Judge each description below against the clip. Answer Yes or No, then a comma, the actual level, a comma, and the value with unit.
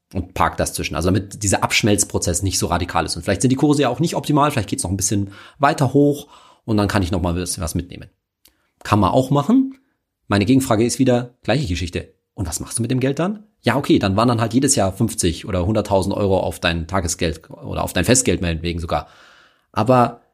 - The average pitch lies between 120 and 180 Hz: No, low, 105 Hz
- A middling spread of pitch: No, wide, 6.2 semitones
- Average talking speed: No, fast, 225 wpm